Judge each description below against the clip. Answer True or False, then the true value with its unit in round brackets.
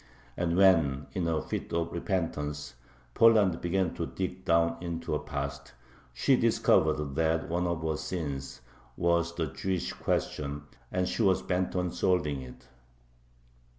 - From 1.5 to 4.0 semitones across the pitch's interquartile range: True (3.5 semitones)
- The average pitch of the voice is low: True (85 Hz)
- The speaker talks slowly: False (145 wpm)